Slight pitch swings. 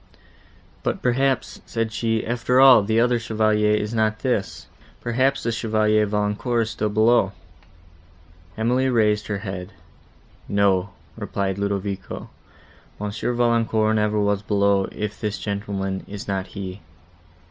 Yes: narrow, 2.3 semitones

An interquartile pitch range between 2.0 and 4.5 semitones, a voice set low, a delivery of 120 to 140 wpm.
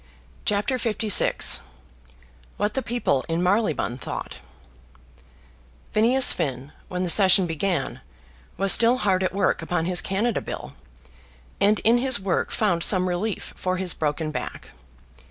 No: average, 3.7 semitones; high, 190 Hz; slow, 135 wpm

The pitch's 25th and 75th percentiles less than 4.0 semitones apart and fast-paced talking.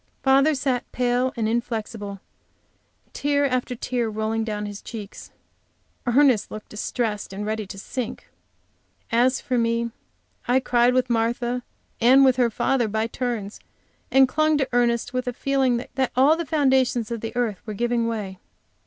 No: average, 2.7 semitones; average, 155 wpm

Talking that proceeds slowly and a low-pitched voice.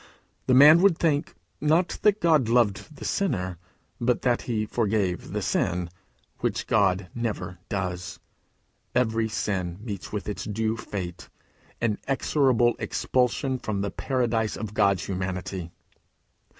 Yes: slow, 125 wpm; low, 110 Hz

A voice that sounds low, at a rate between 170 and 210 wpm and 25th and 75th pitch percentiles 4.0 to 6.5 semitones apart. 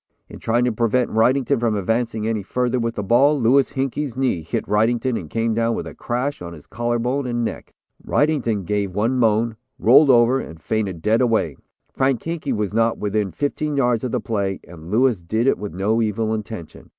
No: low, 115 Hz; average, 200 wpm; average, 3.2 semitones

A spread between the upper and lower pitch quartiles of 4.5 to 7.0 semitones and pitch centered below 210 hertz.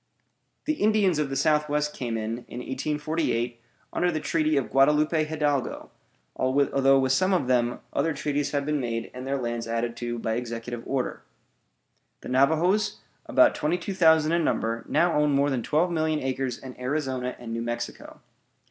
No: average, 4.1 semitones; medium, 140 Hz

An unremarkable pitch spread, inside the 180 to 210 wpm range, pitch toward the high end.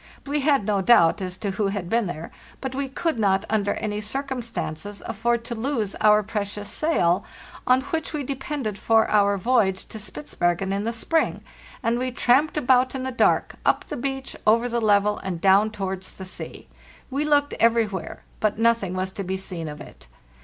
Yes: average, 4.7 semitones; average, 190 wpm; high, 215 Hz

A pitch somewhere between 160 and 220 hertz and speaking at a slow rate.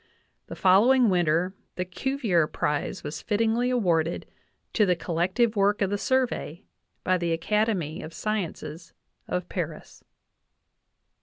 Yes: medium, 185 Hz; slow, 125 wpm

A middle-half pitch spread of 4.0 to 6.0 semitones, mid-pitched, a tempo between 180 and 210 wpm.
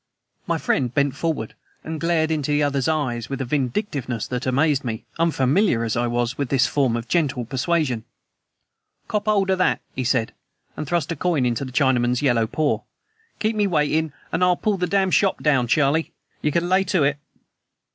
Yes: average, 5.0 semitones; medium, 145 Hz; average, 190 wpm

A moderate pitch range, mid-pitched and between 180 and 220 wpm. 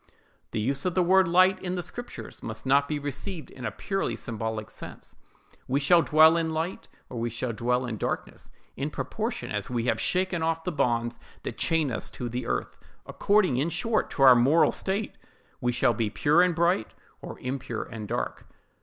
No: wide, 6.6 semitones; medium, 145 Hz; average, 195 wpm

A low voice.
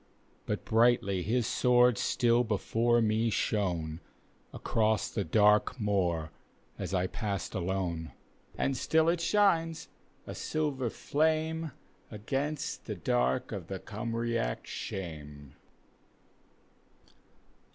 Yes: low, 110 Hz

